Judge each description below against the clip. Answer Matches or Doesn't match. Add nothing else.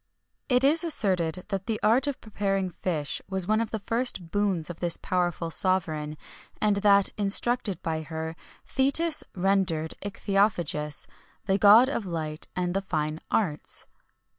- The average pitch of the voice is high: Matches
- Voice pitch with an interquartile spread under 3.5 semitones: Doesn't match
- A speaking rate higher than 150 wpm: Doesn't match